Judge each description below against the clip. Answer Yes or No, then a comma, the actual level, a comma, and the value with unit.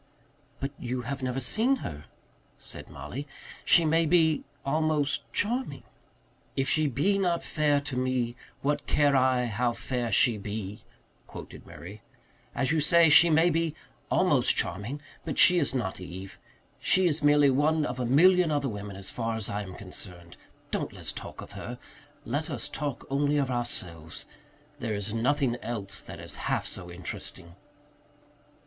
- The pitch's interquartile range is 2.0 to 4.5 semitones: No, wide, 5.6 semitones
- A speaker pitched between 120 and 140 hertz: Yes, low, 135 Hz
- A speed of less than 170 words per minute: Yes, average, 160 wpm